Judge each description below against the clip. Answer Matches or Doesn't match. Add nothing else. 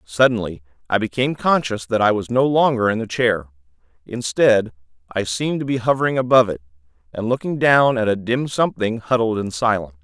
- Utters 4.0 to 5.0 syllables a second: Doesn't match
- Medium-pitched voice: Doesn't match